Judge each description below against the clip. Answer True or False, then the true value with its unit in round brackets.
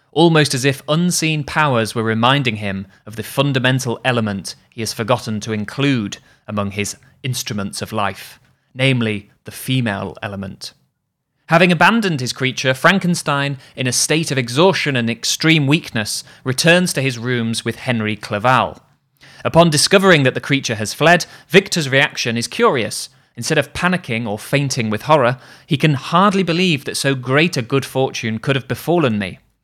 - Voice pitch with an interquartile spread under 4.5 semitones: False (4.9 semitones)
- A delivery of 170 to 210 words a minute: False (160 wpm)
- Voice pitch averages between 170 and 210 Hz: False (130 Hz)